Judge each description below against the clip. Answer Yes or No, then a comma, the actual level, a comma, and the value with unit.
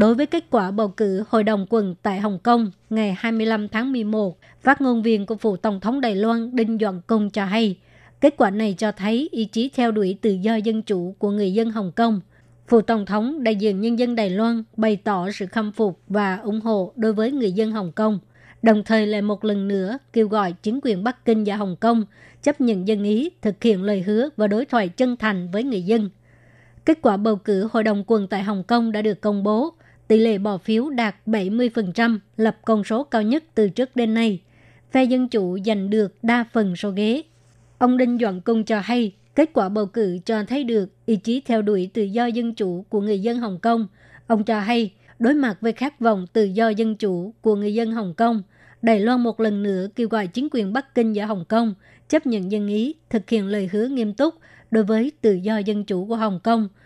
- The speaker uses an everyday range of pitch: No, narrow, 2.0 semitones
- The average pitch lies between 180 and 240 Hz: Yes, high, 220 Hz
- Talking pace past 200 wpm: Yes, average, 230 wpm